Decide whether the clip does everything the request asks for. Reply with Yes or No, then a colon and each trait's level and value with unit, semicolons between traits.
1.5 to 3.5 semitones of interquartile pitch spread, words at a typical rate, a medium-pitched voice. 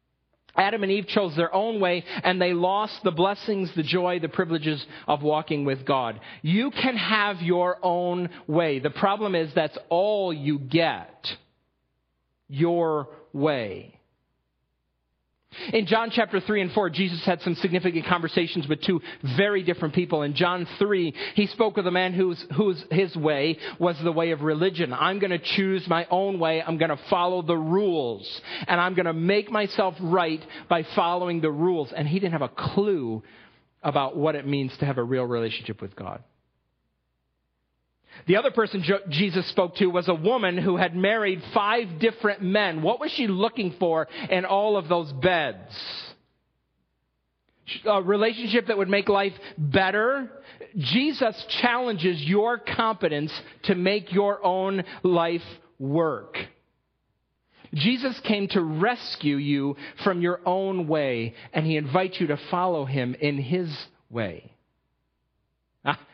No: average, 4.3 semitones; average, 155 wpm; medium, 180 Hz